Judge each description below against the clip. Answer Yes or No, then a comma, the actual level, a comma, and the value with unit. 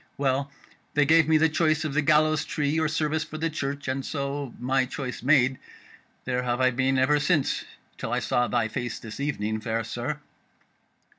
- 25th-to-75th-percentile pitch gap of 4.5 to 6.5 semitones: No, average, 3.5 semitones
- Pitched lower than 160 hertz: Yes, medium, 140 Hz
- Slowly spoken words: No, average, 190 wpm